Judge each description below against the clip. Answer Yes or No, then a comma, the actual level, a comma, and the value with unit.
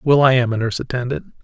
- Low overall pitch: Yes, low, 130 Hz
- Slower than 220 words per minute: No, fast, 250 wpm